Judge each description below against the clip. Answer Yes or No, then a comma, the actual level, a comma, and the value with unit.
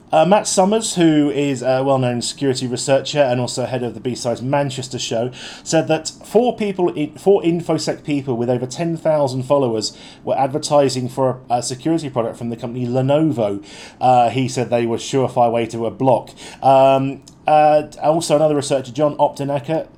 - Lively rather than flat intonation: No, average, 3.4 semitones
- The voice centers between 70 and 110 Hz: No, low, 135 Hz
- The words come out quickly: No, average, 170 wpm